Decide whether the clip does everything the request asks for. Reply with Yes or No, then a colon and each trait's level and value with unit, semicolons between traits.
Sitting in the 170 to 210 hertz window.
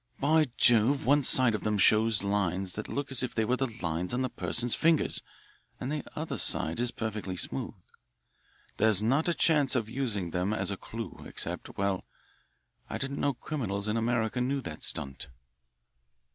No: low, 115 Hz